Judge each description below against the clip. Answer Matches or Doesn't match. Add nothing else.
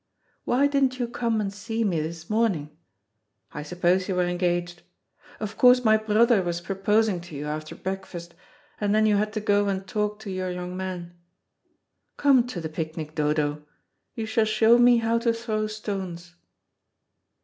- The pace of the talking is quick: Doesn't match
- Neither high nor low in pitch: Doesn't match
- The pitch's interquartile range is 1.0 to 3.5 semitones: Doesn't match